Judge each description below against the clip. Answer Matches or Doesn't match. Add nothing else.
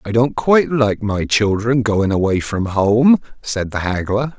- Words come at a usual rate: Matches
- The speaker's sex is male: Matches